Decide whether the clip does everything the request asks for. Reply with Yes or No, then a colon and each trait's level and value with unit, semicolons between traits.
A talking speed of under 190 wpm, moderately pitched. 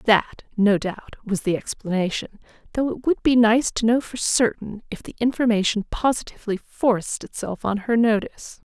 No: average, 165 wpm; high, 220 Hz